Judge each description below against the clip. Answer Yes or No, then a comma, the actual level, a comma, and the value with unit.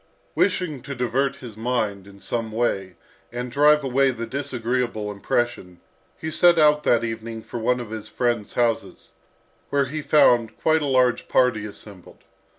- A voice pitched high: No, low, 120 Hz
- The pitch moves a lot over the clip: No, average, 3.8 semitones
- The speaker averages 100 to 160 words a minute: Yes, average, 155 wpm